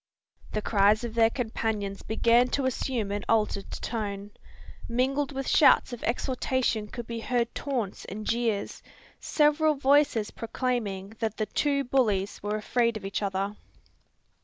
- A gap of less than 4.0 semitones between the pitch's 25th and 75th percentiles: Yes, average, 3.5 semitones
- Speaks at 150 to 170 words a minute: No, average, 140 wpm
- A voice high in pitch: Yes, high, 230 Hz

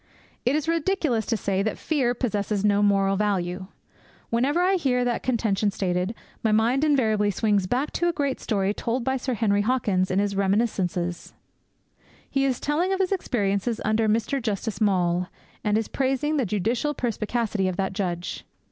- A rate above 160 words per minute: Yes, average, 170 wpm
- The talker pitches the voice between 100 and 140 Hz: No, high, 220 Hz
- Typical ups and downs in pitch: Yes, average, 4.7 semitones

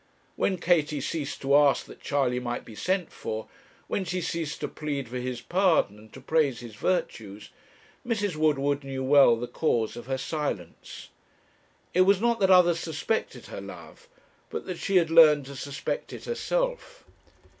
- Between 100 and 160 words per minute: No, average, 170 wpm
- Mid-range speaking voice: Yes, medium, 150 Hz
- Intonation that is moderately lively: No, wide, 5.8 semitones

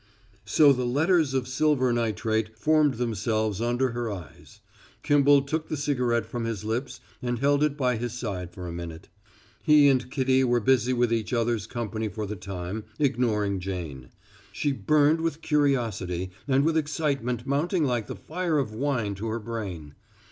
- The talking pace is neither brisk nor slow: Yes, average, 170 wpm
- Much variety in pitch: No, average, 4.7 semitones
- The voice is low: Yes, low, 120 Hz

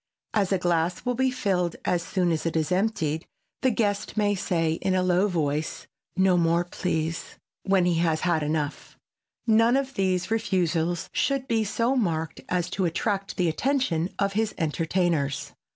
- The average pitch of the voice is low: No, medium, 180 Hz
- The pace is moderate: Yes, average, 160 wpm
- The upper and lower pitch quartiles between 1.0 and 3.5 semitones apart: No, average, 4.1 semitones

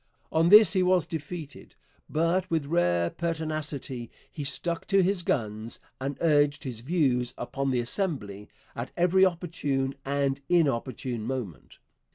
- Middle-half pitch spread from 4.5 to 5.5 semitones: Yes, average, 5.0 semitones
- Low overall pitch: No, medium, 145 Hz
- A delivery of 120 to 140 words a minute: Yes, slow, 135 wpm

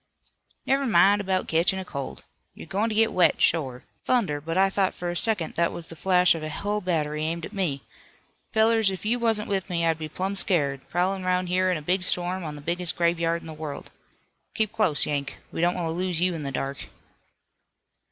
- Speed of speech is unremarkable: No, fast, 215 wpm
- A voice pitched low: No, medium, 180 Hz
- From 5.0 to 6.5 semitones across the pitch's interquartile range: No, average, 3.2 semitones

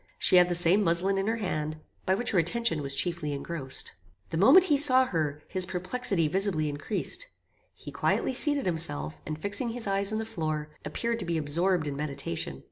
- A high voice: No, medium, 180 Hz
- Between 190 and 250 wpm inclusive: Yes, average, 195 wpm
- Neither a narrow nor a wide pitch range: No, wide, 5.9 semitones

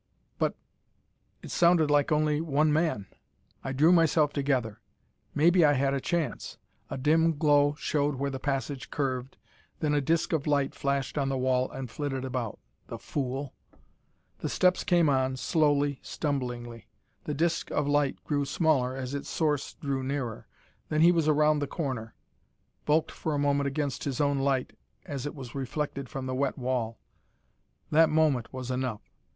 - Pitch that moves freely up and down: No, narrow, 2.6 semitones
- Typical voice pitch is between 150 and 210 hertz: No, medium, 140 Hz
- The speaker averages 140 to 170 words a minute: Yes, average, 165 wpm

